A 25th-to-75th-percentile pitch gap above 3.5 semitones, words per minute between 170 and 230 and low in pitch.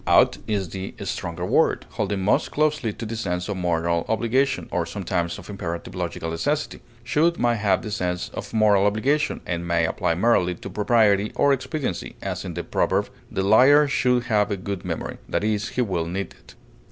Yes: average, 5.0 semitones; average, 190 wpm; low, 105 Hz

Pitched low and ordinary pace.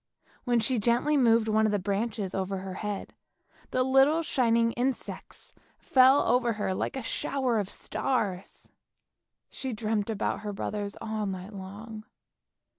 No: high, 220 Hz; average, 145 wpm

